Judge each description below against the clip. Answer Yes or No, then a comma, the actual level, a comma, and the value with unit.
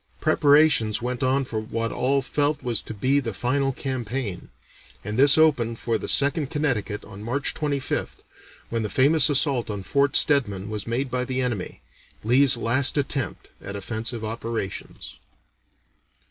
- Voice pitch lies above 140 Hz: No, low, 125 Hz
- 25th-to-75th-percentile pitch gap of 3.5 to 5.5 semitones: Yes, average, 4.0 semitones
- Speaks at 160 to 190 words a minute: No, average, 150 wpm